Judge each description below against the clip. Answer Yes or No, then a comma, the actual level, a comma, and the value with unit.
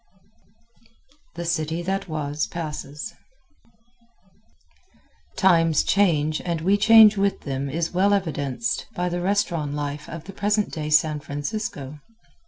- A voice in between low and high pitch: Yes, medium, 165 Hz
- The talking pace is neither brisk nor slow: No, slow, 120 wpm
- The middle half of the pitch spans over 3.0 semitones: Yes, average, 4.6 semitones